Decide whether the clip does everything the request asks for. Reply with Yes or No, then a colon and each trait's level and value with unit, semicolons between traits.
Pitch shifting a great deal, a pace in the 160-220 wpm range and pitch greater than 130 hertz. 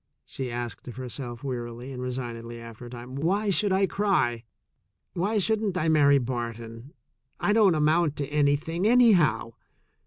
No: wide, 7.0 semitones; average, 150 wpm; medium, 140 Hz